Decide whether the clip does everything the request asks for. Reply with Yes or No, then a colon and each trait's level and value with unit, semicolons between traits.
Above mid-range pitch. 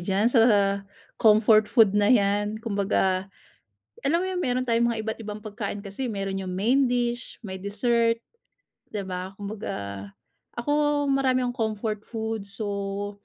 Yes: high, 215 Hz